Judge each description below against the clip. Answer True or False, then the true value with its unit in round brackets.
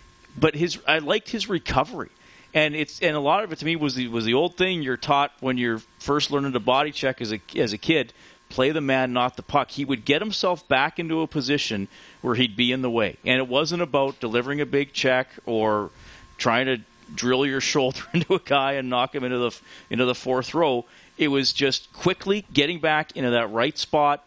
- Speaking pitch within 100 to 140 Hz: True (135 Hz)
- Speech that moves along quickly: True (225 wpm)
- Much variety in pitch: False (3.7 semitones)